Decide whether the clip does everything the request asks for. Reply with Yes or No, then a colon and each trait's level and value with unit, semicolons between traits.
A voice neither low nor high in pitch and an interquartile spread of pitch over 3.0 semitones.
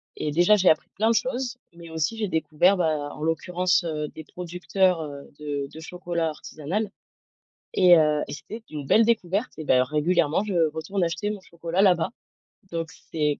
Yes: medium, 170 Hz; average, 3.6 semitones